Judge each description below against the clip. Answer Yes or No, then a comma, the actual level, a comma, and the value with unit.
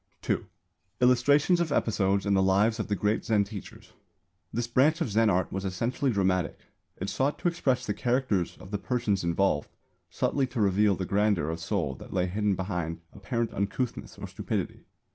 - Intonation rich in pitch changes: No, average, 4.5 semitones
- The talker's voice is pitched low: Yes, low, 105 Hz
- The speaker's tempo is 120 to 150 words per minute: No, average, 180 wpm